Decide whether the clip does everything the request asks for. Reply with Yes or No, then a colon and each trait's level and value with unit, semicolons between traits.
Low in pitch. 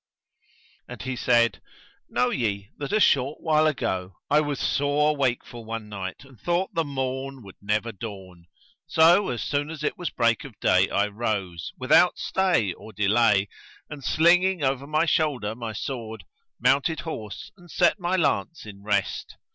Yes: low, 125 Hz